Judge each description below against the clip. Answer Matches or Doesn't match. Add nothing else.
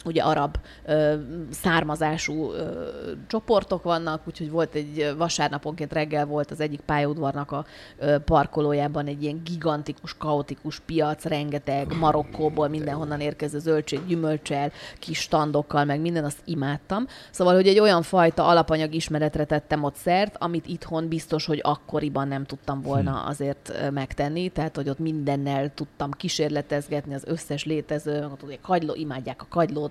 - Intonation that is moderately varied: Doesn't match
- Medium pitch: Matches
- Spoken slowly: Doesn't match